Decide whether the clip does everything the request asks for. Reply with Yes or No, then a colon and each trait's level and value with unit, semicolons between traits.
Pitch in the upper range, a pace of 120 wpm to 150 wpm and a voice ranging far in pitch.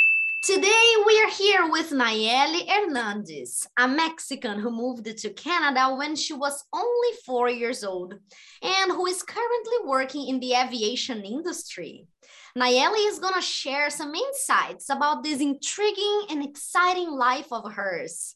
Yes: very high, 290 Hz; average, 145 wpm; wide, 7.1 semitones